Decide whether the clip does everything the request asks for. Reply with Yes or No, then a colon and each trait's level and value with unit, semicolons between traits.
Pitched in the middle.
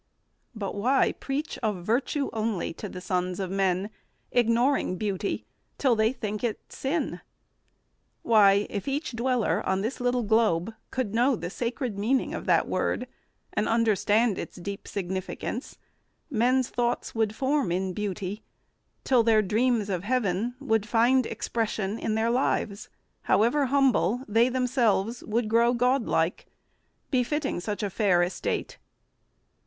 No: high, 225 Hz